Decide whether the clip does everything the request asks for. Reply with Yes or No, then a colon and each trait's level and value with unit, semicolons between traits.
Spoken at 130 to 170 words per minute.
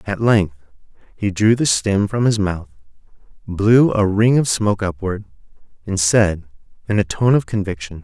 Yes: average, 165 wpm